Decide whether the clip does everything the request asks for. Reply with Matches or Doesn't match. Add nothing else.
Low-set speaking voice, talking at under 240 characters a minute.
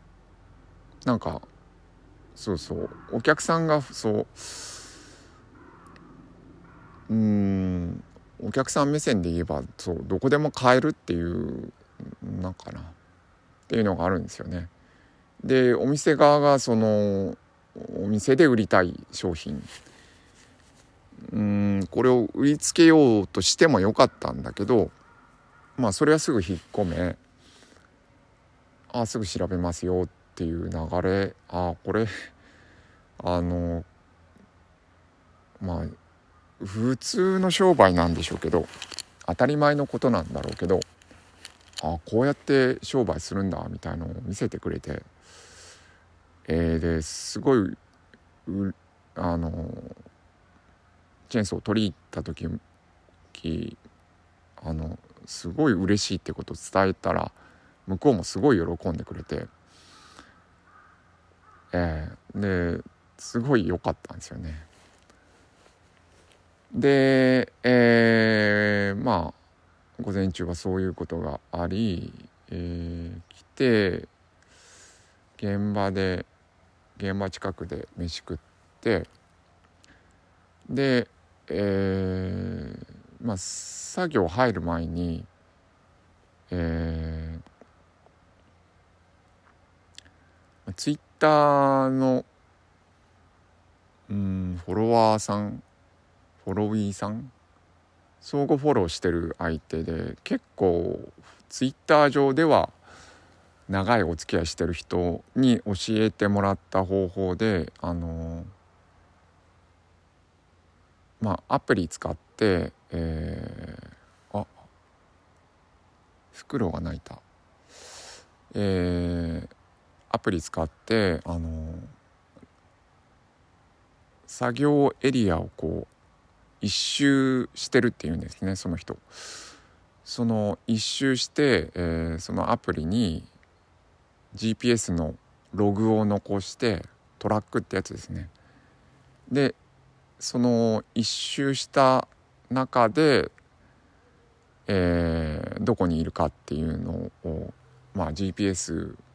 Matches